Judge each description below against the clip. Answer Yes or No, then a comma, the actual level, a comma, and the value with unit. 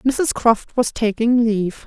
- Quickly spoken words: No, average, 160 wpm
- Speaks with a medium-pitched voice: No, high, 230 Hz